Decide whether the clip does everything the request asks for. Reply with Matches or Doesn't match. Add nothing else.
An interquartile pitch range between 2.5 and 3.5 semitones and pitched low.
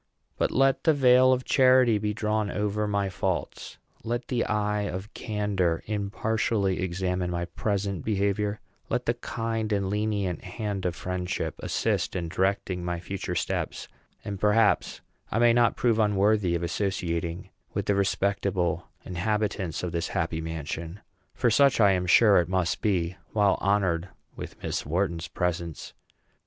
Matches